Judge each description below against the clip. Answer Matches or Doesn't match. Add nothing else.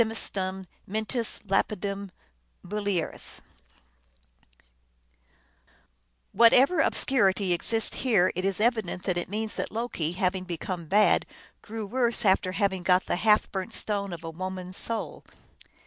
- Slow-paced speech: Matches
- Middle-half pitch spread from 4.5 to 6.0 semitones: Doesn't match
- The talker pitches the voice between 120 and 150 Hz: Doesn't match